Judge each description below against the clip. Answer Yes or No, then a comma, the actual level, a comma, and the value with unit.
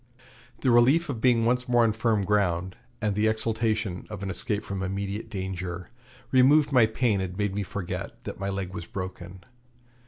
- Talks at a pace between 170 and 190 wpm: Yes, average, 180 wpm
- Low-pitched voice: Yes, low, 105 Hz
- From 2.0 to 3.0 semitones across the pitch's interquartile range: No, average, 3.6 semitones